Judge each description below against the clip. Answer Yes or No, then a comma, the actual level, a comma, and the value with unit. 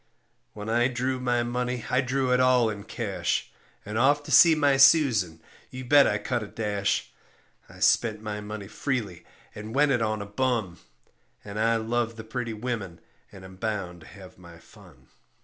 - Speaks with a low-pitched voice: Yes, low, 110 Hz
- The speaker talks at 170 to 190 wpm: Yes, average, 185 wpm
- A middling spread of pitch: Yes, average, 3.7 semitones